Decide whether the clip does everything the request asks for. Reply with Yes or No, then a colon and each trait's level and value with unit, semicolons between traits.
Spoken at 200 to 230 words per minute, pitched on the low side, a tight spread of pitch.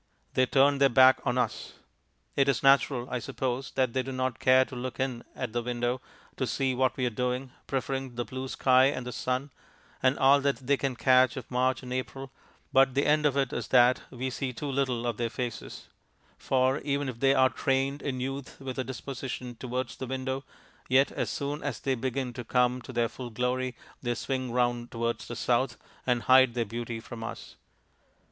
Yes: fast, 205 wpm; low, 130 Hz; narrow, 1.5 semitones